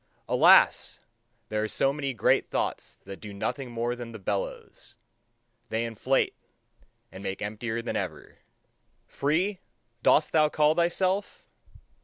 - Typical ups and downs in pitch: No, wide, 5.8 semitones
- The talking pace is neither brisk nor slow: No, slow, 130 wpm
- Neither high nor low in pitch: No, low, 120 Hz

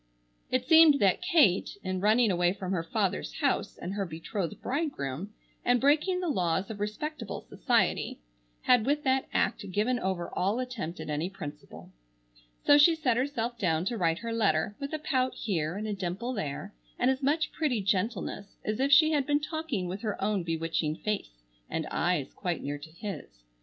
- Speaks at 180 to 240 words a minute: Yes, average, 185 wpm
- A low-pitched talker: No, high, 210 Hz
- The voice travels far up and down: Yes, wide, 6.9 semitones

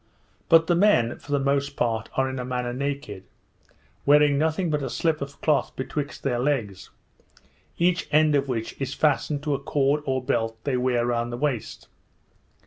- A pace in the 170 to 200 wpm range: Yes, average, 180 wpm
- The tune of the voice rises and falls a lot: No, average, 3.3 semitones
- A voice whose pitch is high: No, medium, 140 Hz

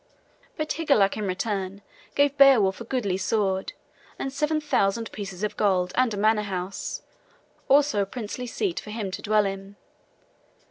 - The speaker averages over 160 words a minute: No, average, 155 wpm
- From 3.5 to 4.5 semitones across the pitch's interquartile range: No, average, 4.9 semitones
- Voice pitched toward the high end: Yes, high, 210 Hz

